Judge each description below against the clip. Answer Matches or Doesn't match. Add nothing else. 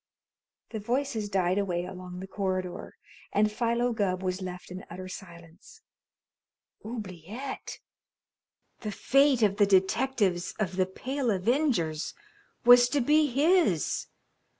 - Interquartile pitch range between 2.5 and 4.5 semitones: Doesn't match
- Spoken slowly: Matches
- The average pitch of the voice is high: Matches